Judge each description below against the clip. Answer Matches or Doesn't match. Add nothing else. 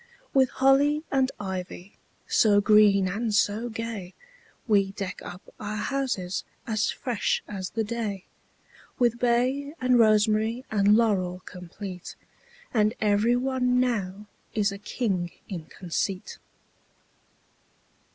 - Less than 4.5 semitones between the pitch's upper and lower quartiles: Matches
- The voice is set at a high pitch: Matches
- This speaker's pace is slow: Matches